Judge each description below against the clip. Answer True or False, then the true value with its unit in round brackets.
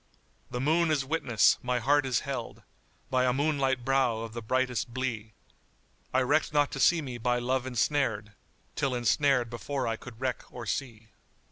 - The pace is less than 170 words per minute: False (180 wpm)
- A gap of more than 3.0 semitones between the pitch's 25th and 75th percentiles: False (2.5 semitones)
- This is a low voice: True (130 Hz)